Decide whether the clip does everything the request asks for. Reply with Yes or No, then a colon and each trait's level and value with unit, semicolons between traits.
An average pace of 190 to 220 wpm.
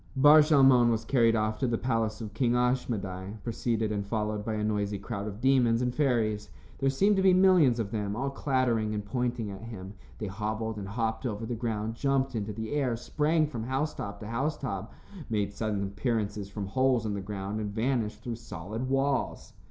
Yes: average, 195 wpm